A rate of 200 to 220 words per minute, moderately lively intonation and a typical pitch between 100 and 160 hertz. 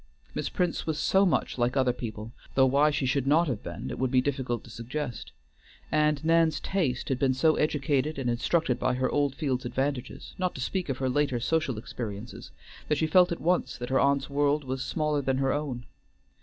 Yes: fast, 205 wpm; average, 3.2 semitones; low, 135 Hz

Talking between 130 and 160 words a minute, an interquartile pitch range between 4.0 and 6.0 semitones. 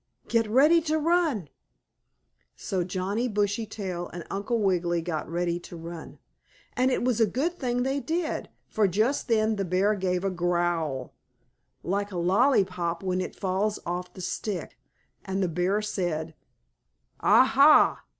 Yes: average, 150 wpm; average, 4.6 semitones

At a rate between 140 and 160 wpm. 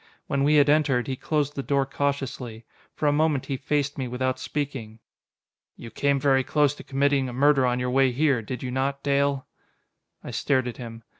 No: average, 200 wpm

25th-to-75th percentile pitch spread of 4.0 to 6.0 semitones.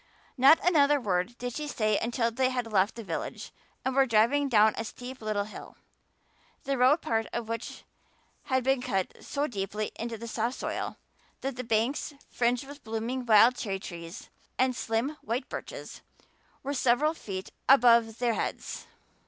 No: average, 3.2 semitones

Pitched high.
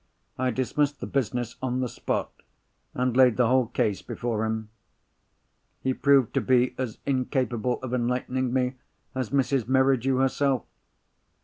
No: low, 125 Hz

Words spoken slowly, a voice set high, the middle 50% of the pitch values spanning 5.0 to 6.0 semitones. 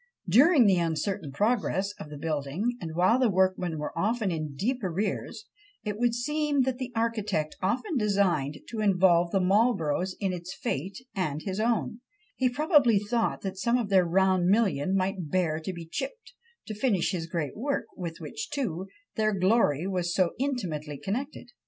No: average, 170 wpm; high, 195 Hz; average, 5.3 semitones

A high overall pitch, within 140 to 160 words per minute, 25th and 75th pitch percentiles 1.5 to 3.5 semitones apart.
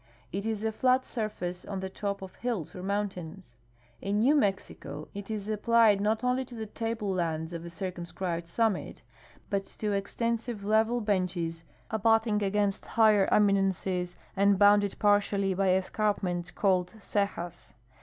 Yes: high, 200 Hz; average, 150 wpm; average, 2.8 semitones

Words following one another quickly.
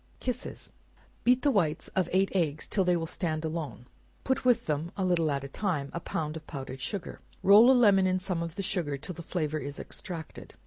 Yes: fast, 215 wpm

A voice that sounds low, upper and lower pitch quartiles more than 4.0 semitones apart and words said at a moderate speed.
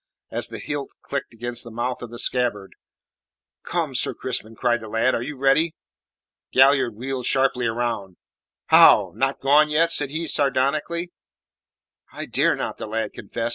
No: low, 130 Hz; average, 3.3 semitones; average, 160 wpm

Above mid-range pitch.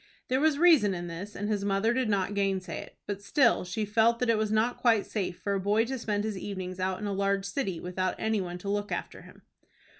Yes: high, 205 Hz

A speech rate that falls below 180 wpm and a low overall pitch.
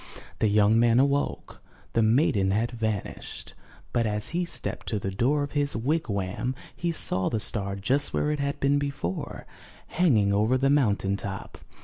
Yes: average, 170 wpm; low, 115 Hz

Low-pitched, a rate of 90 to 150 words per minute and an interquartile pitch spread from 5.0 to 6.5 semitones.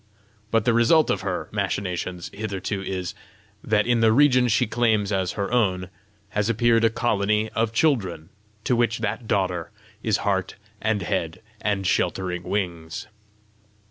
No: low, 105 Hz; average, 145 wpm; average, 3.5 semitones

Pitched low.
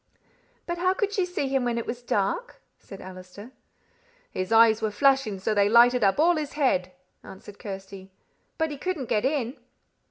No: high, 235 Hz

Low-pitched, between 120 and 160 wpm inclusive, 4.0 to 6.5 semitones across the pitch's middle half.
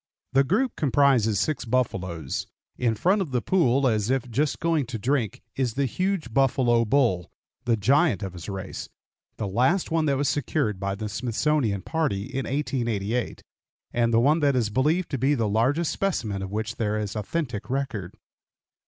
No: low, 125 Hz; average, 175 wpm; average, 5.1 semitones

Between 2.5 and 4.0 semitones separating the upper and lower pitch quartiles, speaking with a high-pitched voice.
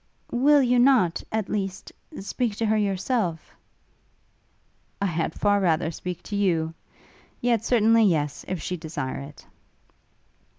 No: wide, 5.4 semitones; high, 200 Hz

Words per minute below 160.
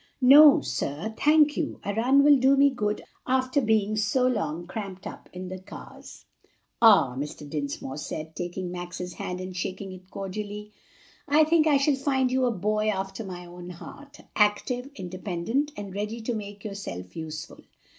No: average, 165 wpm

